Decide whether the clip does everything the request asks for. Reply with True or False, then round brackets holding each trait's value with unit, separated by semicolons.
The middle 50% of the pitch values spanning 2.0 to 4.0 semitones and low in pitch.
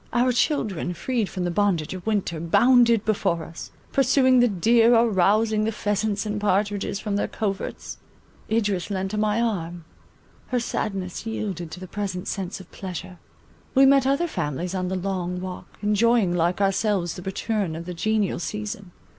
False (3.5 semitones; 200 Hz)